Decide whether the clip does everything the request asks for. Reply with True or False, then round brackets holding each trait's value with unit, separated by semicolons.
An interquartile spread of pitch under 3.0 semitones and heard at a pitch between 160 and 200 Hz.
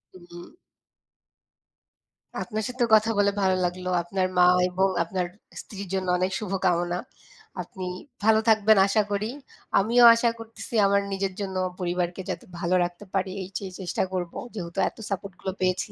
True (2.4 semitones; 190 Hz)